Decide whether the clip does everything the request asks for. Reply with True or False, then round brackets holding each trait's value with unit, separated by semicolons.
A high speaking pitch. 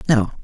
False (125 Hz)